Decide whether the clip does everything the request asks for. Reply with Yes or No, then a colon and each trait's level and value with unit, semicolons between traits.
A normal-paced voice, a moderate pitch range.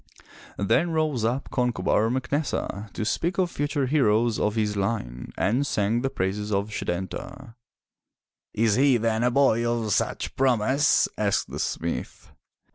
Yes: average, 150 wpm; average, 4.4 semitones